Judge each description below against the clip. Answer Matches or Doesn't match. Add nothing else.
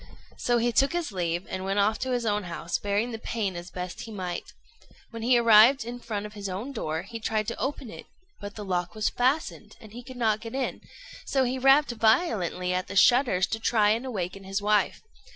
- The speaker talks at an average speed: Doesn't match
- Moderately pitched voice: Doesn't match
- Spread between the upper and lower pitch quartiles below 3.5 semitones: Doesn't match